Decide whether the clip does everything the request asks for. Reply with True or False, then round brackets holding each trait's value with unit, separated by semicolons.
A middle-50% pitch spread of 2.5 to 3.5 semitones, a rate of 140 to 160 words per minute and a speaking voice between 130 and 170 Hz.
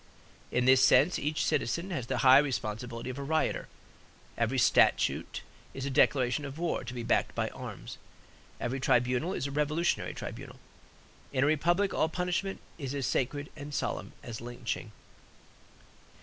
False (3.9 semitones; 155 wpm; 135 Hz)